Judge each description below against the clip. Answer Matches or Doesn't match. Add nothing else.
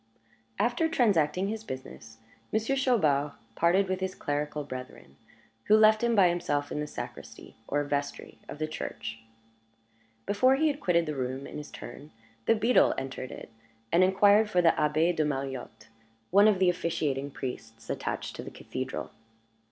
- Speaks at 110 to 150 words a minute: Doesn't match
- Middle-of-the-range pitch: Matches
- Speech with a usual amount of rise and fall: Doesn't match